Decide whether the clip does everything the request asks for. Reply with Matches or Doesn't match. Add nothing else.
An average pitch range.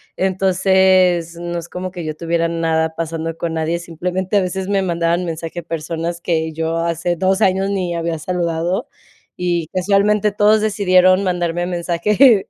Doesn't match